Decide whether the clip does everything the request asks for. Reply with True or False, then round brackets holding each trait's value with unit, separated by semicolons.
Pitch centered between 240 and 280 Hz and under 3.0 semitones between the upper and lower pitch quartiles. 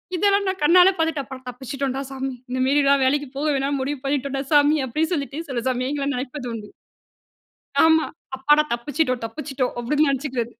True (275 Hz; 2.6 semitones)